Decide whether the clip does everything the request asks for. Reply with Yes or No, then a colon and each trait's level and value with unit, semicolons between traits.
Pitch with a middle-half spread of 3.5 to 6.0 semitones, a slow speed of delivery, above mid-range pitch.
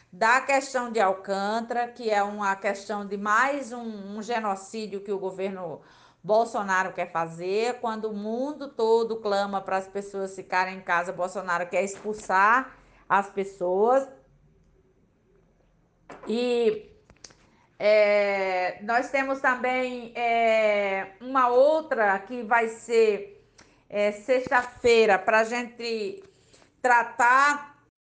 Yes: average, 3.8 semitones; slow, 110 wpm; high, 220 Hz